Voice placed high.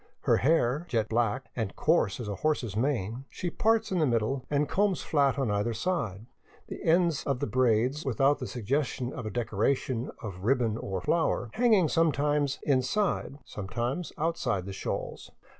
No: low, 130 Hz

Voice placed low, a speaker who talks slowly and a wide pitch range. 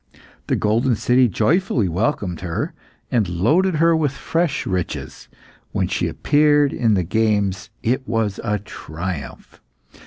Yes: low, 110 Hz; slow, 130 wpm; wide, 7.5 semitones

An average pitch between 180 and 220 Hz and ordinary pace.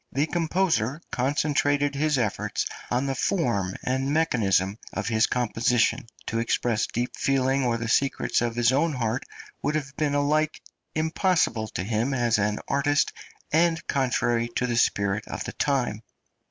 No: low, 130 Hz; average, 155 wpm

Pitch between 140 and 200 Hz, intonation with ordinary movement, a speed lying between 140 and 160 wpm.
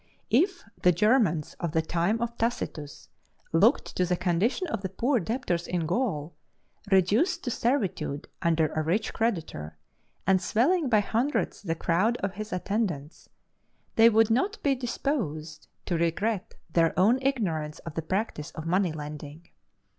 No: high, 190 Hz; wide, 6.1 semitones; average, 150 wpm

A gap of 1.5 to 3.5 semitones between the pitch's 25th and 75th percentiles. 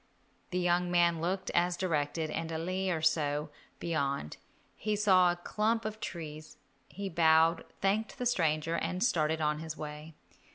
Yes: average, 3.1 semitones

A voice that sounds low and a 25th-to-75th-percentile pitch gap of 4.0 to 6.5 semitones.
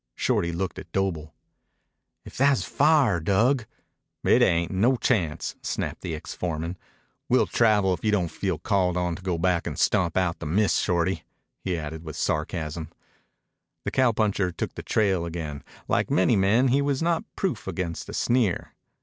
Yes: very low, 95 Hz; average, 4.5 semitones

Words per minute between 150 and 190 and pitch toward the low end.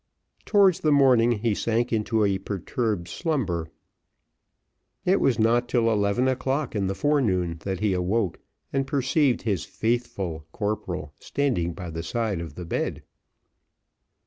No: average, 140 wpm; low, 110 Hz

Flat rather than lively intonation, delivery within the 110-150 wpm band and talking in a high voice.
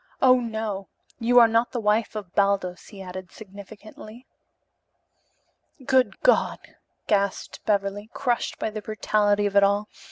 Yes: narrow, 2.3 semitones; slow, 135 wpm; high, 210 Hz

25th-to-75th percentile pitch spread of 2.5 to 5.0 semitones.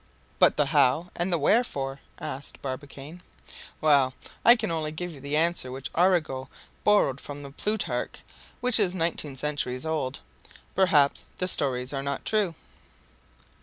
Yes: average, 4.5 semitones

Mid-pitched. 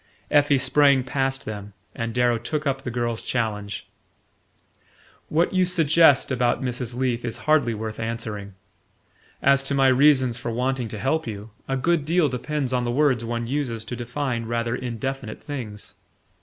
No: low, 125 Hz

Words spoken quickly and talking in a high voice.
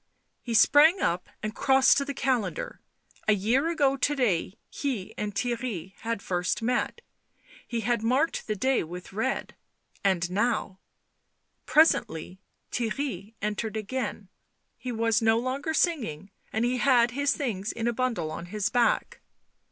No: average, 150 wpm; high, 230 Hz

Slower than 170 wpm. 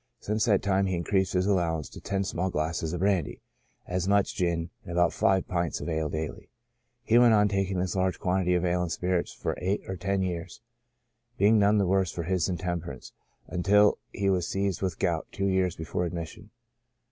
No: average, 195 wpm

